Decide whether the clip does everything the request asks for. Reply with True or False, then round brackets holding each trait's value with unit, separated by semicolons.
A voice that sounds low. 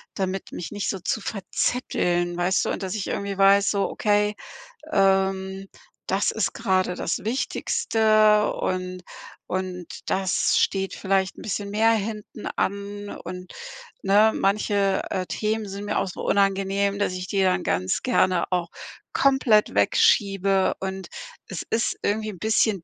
False (195 Hz)